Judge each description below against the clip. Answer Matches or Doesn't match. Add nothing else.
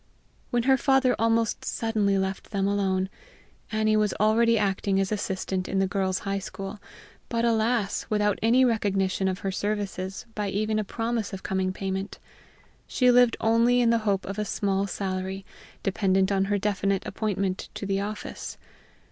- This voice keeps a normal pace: Matches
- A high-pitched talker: Matches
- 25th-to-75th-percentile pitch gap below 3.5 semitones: Matches